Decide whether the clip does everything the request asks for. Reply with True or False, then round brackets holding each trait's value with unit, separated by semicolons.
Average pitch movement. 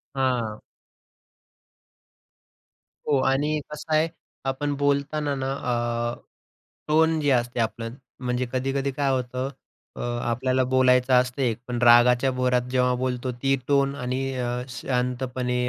False (1.8 semitones)